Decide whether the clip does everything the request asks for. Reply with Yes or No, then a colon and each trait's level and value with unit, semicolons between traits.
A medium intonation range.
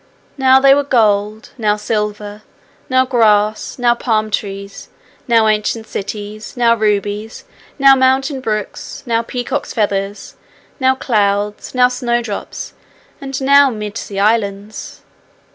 Yes: average, 3.4 semitones